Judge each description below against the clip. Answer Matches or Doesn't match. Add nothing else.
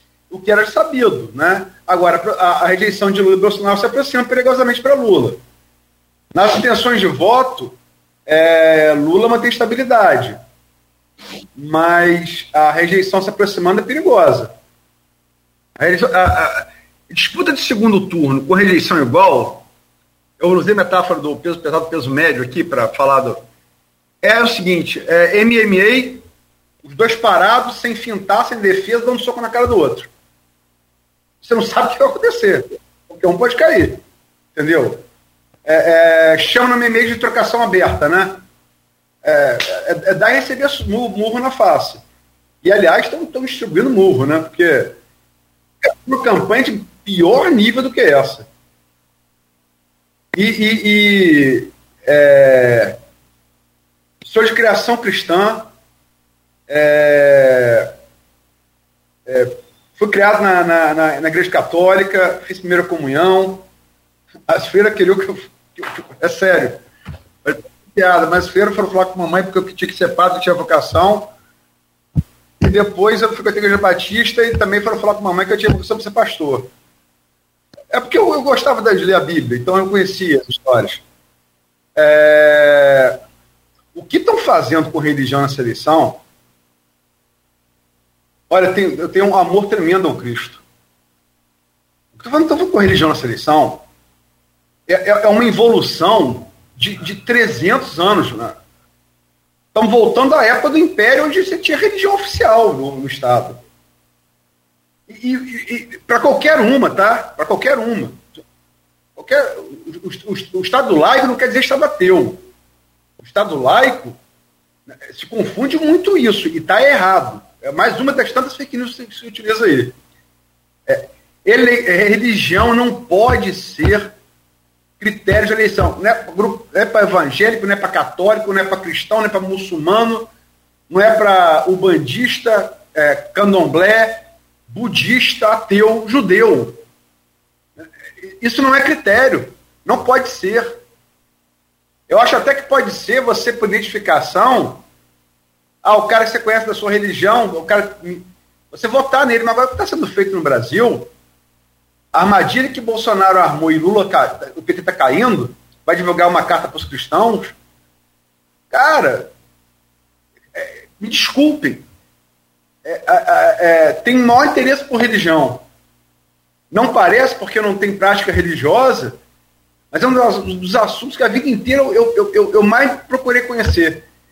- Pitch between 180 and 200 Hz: Matches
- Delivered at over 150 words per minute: Doesn't match